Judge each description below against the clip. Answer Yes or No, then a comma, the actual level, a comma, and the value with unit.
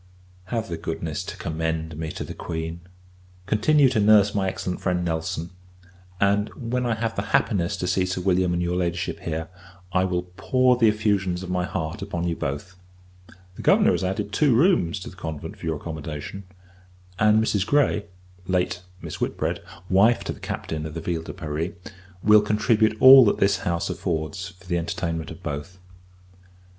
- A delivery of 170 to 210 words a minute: Yes, average, 180 wpm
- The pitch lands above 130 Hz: No, very low, 90 Hz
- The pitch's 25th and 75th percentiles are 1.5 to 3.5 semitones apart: No, average, 4.2 semitones